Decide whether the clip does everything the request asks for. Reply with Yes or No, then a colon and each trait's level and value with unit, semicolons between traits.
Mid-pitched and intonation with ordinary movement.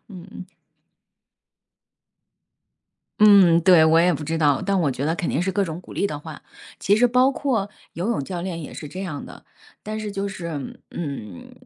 Yes: medium, 175 Hz; average, 4.0 semitones